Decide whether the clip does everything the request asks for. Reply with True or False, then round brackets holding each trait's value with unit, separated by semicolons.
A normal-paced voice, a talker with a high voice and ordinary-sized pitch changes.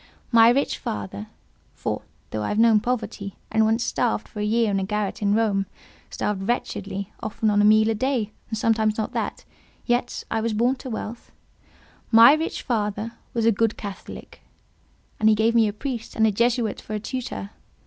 False (180 wpm; 220 Hz; 2.0 semitones)